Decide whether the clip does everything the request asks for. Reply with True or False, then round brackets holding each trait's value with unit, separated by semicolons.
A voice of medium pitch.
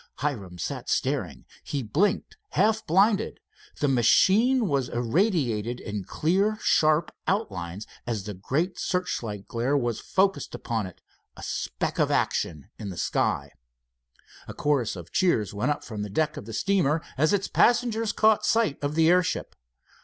True (145 Hz)